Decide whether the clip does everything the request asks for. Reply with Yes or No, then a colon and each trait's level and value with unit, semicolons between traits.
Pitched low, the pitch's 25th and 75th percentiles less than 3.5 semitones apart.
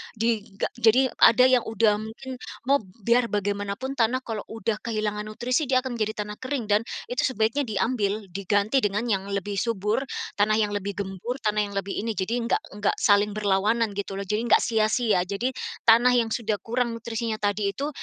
No: high, 215 Hz; narrow, 2.6 semitones